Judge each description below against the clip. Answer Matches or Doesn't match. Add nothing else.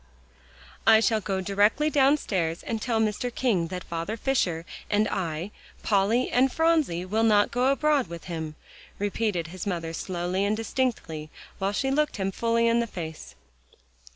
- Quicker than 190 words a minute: Doesn't match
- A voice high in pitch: Matches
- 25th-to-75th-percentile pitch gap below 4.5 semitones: Doesn't match